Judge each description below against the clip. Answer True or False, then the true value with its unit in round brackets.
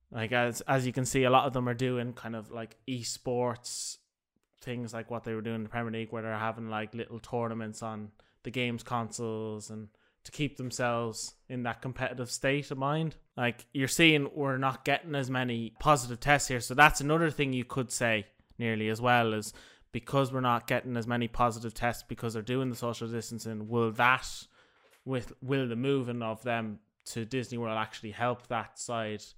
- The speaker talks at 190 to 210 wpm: True (200 wpm)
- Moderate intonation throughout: False (2.3 semitones)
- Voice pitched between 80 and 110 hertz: False (120 Hz)